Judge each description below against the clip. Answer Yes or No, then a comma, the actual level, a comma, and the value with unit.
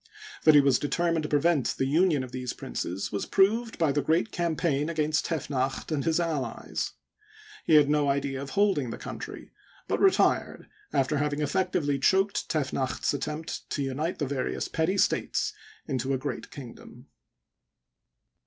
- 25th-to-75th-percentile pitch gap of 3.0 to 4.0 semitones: Yes, average, 3.4 semitones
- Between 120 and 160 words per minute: Yes, average, 155 wpm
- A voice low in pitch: No, medium, 150 Hz